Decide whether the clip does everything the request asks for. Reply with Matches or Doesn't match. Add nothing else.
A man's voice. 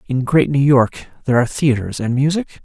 Matches